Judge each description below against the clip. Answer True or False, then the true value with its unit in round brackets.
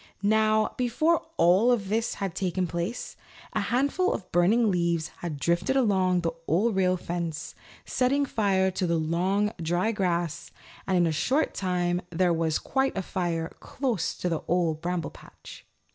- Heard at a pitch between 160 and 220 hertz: True (185 Hz)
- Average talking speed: True (160 wpm)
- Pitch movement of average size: True (4.2 semitones)